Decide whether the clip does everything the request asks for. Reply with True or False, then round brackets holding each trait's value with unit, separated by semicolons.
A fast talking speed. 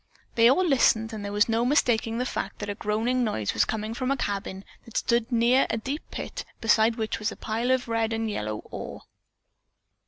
True (210 wpm)